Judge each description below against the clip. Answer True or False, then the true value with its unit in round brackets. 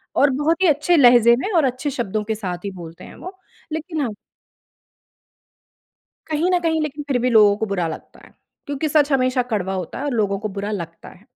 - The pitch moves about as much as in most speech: False (6.8 semitones)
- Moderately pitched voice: False (255 Hz)